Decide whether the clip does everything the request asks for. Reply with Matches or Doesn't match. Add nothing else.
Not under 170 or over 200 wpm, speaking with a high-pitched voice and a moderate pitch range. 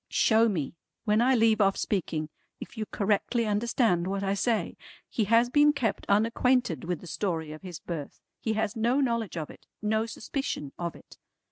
Matches